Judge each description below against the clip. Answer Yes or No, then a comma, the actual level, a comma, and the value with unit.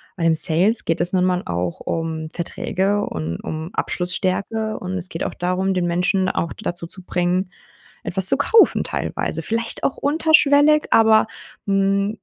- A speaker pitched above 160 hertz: Yes, medium, 185 Hz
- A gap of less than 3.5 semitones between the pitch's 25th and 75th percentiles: No, average, 3.9 semitones